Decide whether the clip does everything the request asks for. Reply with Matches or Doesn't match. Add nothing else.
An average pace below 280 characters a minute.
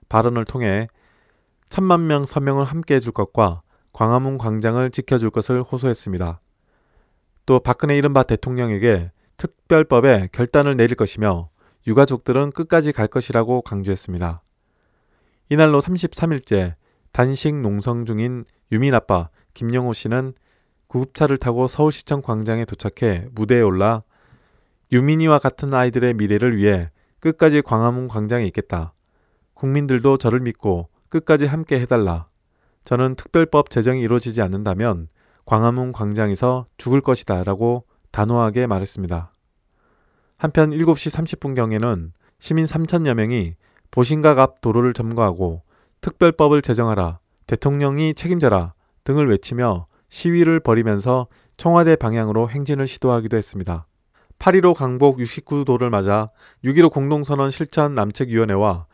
Doesn't match